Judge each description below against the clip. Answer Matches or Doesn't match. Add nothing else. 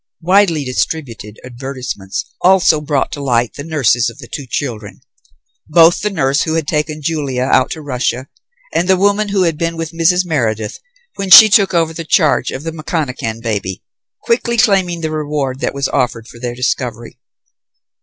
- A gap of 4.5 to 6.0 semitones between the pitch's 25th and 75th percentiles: Matches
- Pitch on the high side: Doesn't match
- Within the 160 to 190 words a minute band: Matches